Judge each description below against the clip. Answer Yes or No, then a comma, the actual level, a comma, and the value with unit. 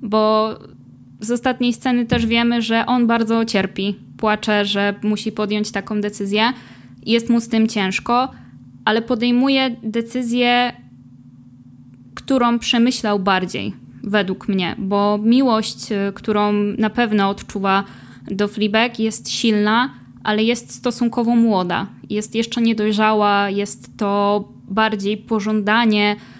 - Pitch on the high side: Yes, high, 215 Hz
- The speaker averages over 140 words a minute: No, average, 115 wpm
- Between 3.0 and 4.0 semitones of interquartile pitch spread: No, narrow, 2.6 semitones